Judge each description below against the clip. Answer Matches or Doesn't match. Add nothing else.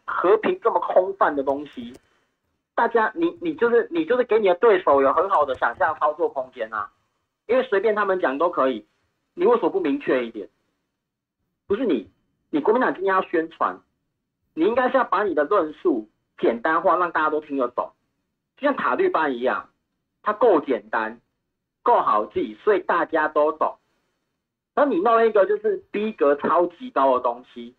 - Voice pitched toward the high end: Matches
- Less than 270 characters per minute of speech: Matches